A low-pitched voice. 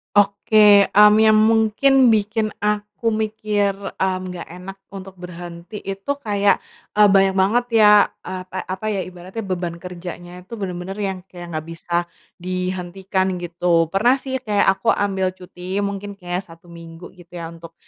No: high, 190 Hz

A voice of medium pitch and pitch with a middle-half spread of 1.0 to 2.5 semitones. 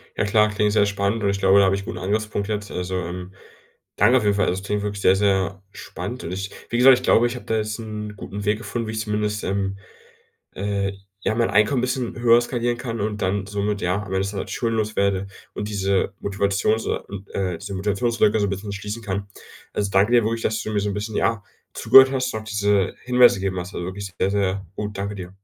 No: low, 105 Hz; narrow, 1.9 semitones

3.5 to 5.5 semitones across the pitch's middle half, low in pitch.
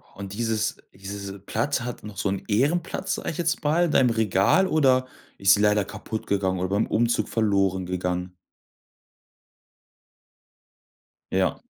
Yes: average, 4.4 semitones; low, 105 Hz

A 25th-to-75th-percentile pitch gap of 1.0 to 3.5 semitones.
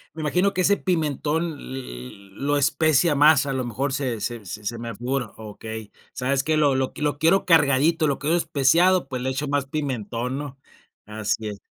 No: average, 4.2 semitones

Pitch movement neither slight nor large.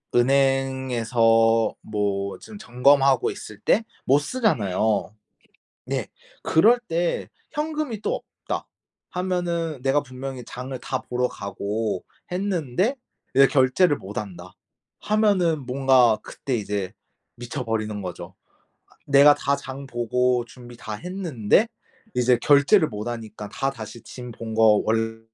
Yes: average, 4.6 semitones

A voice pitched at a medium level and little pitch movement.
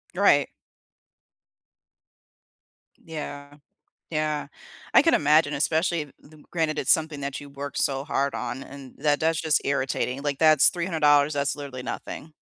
Yes: medium, 145 Hz; narrow, 2.0 semitones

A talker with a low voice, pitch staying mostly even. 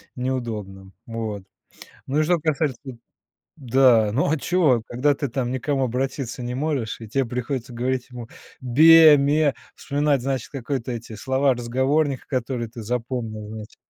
No: low, 130 Hz; average, 3.2 semitones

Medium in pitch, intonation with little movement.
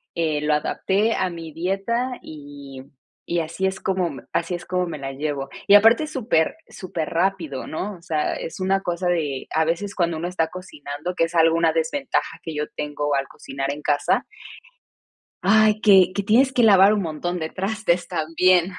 No: medium, 170 Hz; average, 3.8 semitones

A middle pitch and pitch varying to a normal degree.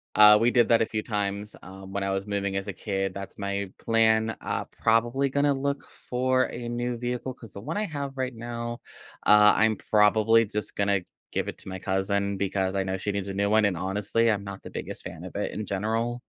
No: low, 105 Hz; average, 3.0 semitones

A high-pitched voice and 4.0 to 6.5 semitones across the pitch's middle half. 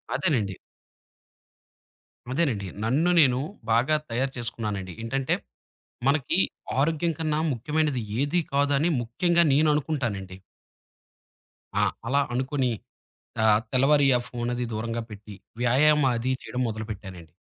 No: low, 130 Hz; average, 4.8 semitones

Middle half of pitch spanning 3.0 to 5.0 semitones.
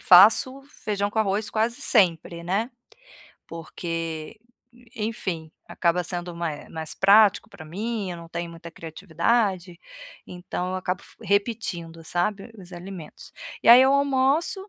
Yes: average, 4.5 semitones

